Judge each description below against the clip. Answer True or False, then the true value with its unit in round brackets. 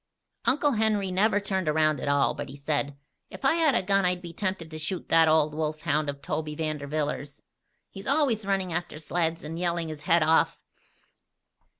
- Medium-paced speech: True (190 wpm)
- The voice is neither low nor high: True (165 Hz)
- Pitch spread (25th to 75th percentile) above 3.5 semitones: True (4.1 semitones)